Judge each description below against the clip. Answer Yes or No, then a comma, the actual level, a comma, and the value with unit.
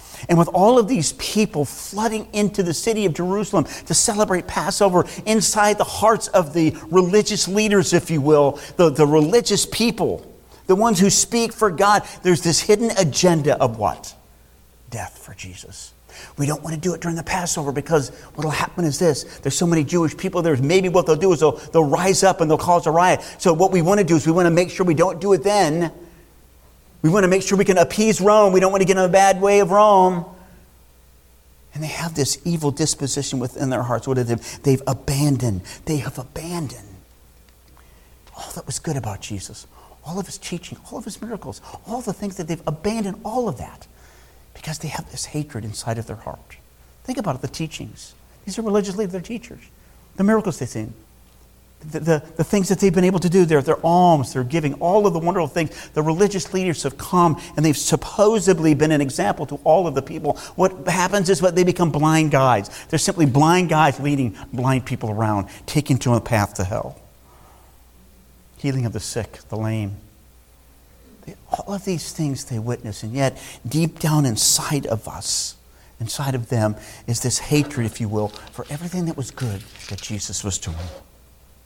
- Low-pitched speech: No, medium, 155 Hz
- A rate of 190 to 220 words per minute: Yes, average, 200 wpm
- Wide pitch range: Yes, wide, 8.5 semitones